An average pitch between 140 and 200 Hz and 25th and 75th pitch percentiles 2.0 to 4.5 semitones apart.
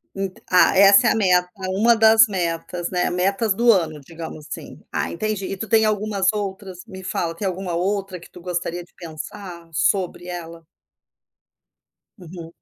Yes: medium, 185 Hz; average, 2.8 semitones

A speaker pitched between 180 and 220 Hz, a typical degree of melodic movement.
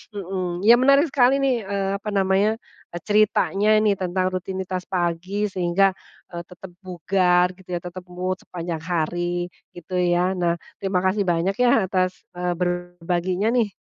No: medium, 185 Hz; narrow, 2.0 semitones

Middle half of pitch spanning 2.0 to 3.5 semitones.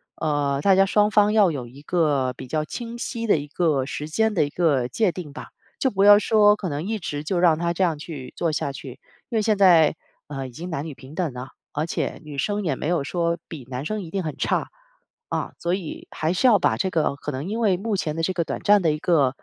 No: average, 5.3 semitones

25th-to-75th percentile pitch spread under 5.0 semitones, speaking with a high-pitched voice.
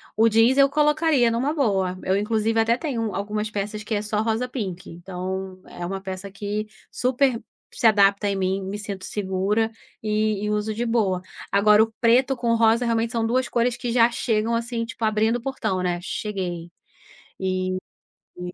Yes: average, 3.1 semitones; high, 215 Hz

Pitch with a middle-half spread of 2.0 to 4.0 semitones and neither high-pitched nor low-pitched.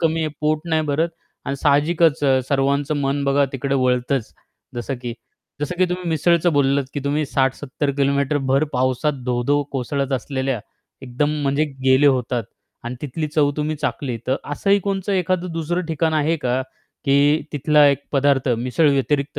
Yes: narrow, 2.4 semitones; medium, 145 Hz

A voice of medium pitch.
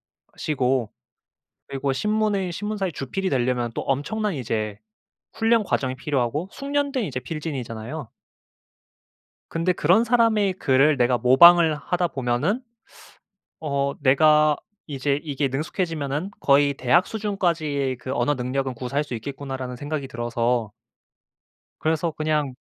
Yes: medium, 145 Hz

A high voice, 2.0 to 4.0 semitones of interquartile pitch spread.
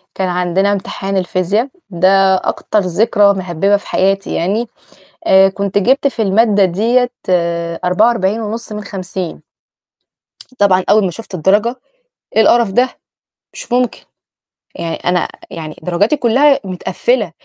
Yes: high, 200 Hz; average, 3.5 semitones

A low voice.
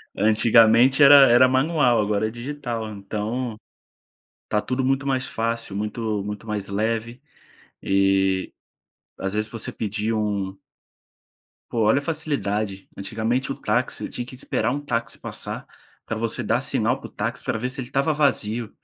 Yes: low, 115 Hz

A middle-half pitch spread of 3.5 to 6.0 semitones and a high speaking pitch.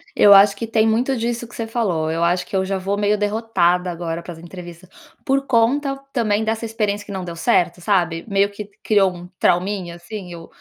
Yes: average, 4.1 semitones; high, 200 Hz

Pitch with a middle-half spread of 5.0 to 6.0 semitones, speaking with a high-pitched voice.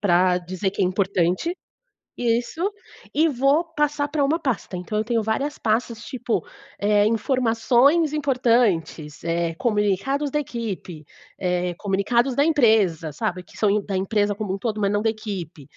Yes: wide, 5.5 semitones; high, 215 Hz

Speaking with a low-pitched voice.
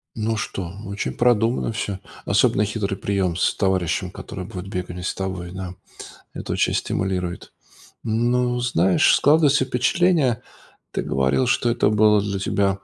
Yes: low, 100 Hz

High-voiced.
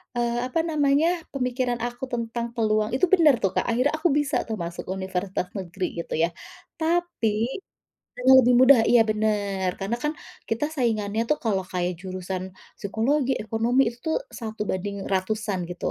Yes: high, 225 Hz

